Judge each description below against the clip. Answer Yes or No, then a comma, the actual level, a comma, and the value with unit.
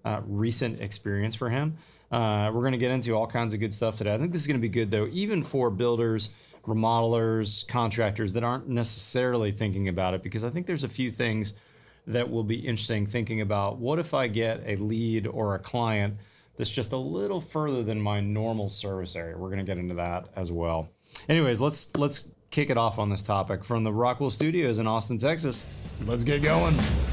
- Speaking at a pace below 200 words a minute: No, fast, 205 wpm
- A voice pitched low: Yes, low, 115 Hz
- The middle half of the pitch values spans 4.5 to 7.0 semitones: No, average, 3.2 semitones